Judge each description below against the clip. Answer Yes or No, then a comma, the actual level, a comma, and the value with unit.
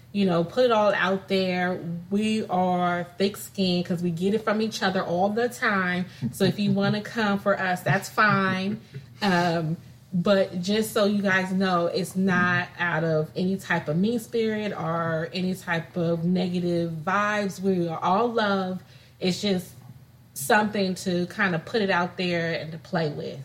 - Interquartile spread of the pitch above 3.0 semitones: No, average, 2.7 semitones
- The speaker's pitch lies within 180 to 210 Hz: Yes, medium, 185 Hz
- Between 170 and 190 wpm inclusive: Yes, average, 180 wpm